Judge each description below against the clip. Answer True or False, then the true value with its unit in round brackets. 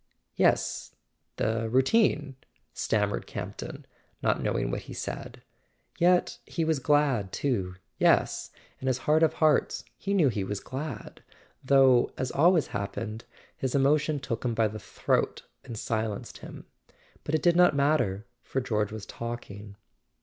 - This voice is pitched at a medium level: False (130 Hz)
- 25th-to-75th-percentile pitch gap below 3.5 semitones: False (5.5 semitones)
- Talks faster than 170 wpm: False (145 wpm)